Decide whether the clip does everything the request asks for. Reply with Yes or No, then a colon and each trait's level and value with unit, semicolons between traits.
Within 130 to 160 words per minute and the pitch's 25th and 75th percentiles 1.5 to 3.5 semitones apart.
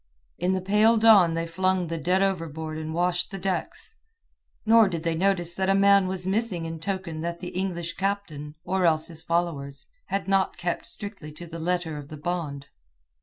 No: average, 190 wpm; average, 2.8 semitones